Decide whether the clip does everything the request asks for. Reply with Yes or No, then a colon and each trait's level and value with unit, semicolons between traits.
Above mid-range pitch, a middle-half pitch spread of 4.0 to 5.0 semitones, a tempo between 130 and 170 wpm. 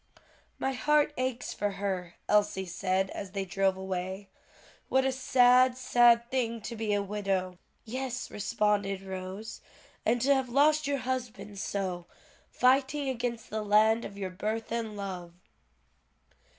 Yes: high, 215 Hz; average, 4.5 semitones; average, 140 wpm